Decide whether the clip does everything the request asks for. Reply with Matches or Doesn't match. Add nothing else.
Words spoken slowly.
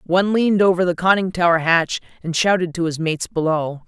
Doesn't match